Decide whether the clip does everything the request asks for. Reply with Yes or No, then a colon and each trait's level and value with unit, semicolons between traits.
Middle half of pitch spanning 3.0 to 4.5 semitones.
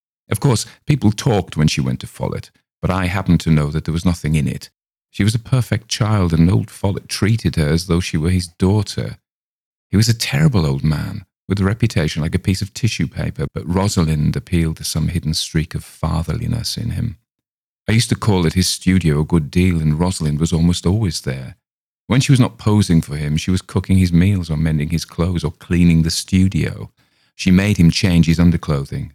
Yes: average, 3.9 semitones